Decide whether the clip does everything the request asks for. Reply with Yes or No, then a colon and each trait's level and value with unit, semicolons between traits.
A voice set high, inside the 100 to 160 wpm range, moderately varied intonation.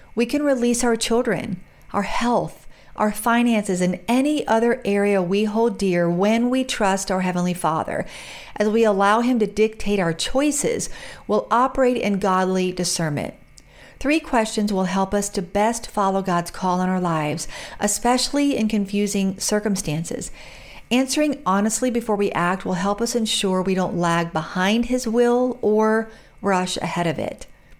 Yes: high, 205 Hz; average, 155 wpm; average, 4.1 semitones